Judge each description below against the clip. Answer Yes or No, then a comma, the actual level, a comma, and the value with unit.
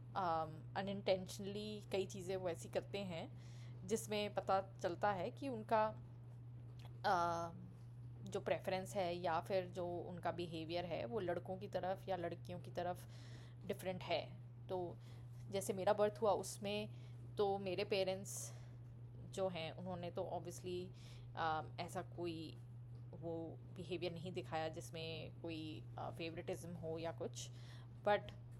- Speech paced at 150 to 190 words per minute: No, average, 135 wpm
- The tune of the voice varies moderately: No, wide, 7.0 semitones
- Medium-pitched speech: Yes, medium, 160 Hz